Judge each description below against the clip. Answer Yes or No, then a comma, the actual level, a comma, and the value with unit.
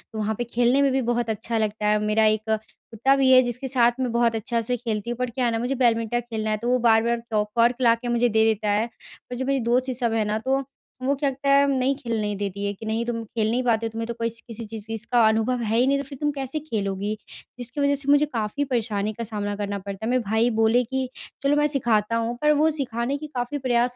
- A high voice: Yes, high, 235 Hz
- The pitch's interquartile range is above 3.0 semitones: No, average, 2.7 semitones